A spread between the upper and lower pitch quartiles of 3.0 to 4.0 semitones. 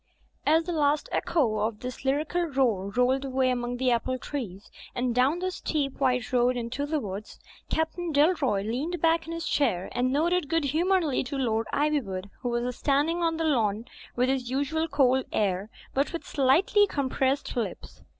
No: average, 4.5 semitones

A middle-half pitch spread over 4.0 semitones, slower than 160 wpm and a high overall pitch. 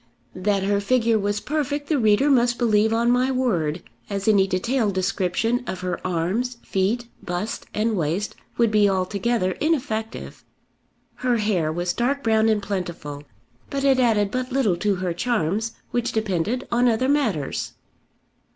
Yes: average, 4.6 semitones; average, 150 wpm; high, 215 Hz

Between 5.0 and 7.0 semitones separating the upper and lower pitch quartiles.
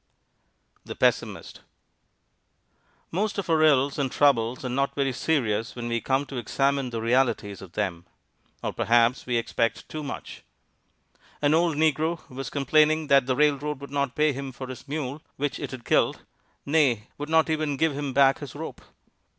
No: average, 3.2 semitones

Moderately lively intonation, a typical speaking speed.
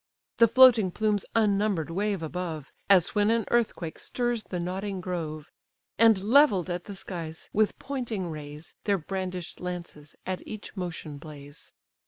Yes: average, 4.2 semitones; average, 145 wpm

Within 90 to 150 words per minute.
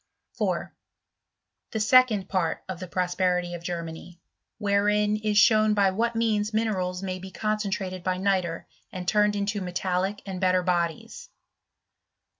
Yes: average, 140 wpm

